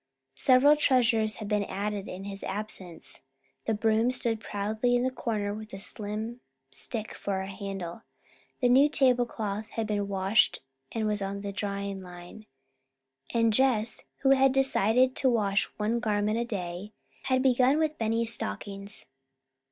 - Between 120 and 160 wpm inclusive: Yes, average, 150 wpm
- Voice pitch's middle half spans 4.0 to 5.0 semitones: No, average, 3.4 semitones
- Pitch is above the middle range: Yes, high, 215 Hz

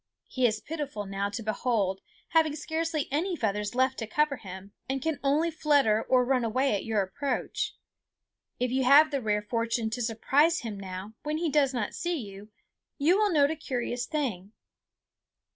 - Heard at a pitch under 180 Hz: No, very high, 255 Hz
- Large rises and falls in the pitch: Yes, wide, 5.9 semitones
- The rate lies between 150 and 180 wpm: Yes, average, 175 wpm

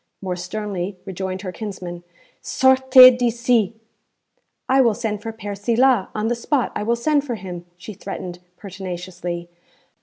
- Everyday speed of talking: Yes, average, 145 wpm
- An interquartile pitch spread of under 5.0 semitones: Yes, average, 4.5 semitones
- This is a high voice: Yes, high, 210 Hz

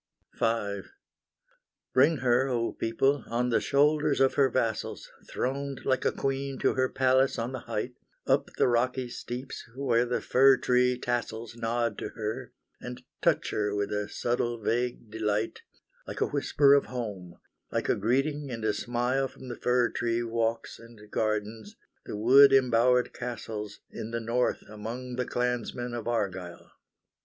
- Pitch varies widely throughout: No, narrow, 2.5 semitones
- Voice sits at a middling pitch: No, low, 120 Hz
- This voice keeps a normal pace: Yes, average, 155 wpm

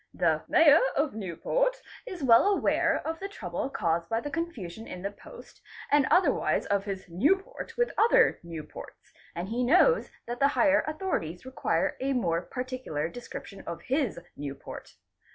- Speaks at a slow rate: No, average, 155 wpm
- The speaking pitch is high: Yes, high, 245 Hz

